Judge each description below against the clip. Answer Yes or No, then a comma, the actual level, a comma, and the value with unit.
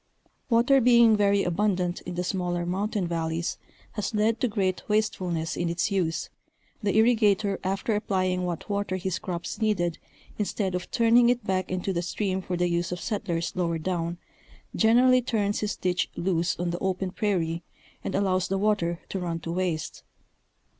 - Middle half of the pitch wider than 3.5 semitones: No, average, 3.2 semitones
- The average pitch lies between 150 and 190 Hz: Yes, medium, 185 Hz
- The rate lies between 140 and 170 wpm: Yes, average, 165 wpm